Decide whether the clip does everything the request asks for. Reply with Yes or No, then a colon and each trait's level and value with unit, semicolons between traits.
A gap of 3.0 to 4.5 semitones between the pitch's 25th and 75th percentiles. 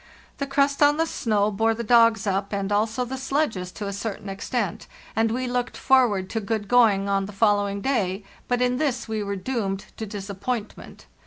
Yes: average, 3.8 semitones